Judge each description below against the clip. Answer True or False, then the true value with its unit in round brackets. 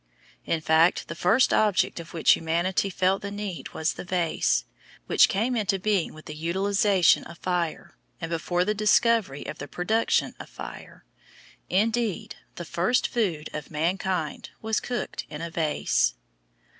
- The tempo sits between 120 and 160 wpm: True (155 wpm)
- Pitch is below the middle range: False (185 Hz)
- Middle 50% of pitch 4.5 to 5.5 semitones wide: False (4.0 semitones)